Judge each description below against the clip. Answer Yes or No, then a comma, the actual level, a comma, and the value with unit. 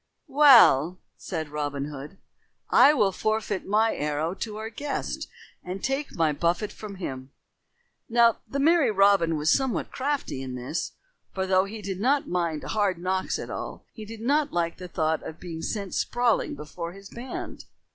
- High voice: Yes, high, 195 Hz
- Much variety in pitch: Yes, wide, 5.8 semitones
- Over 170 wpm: No, average, 165 wpm